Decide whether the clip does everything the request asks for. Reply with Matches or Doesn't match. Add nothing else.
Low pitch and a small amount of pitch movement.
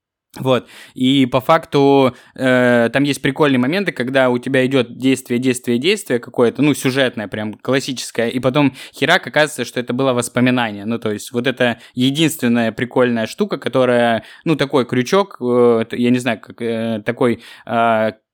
Matches